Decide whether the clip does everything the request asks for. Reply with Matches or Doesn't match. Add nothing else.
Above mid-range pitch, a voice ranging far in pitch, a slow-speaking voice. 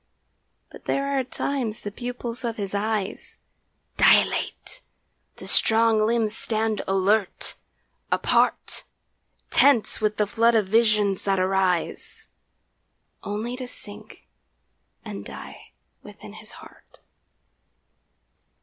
Doesn't match